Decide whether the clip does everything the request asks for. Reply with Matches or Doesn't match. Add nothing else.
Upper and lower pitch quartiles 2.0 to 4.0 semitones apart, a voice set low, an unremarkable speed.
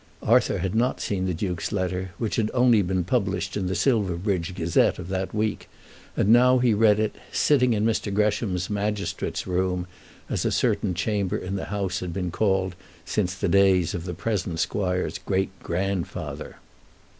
Matches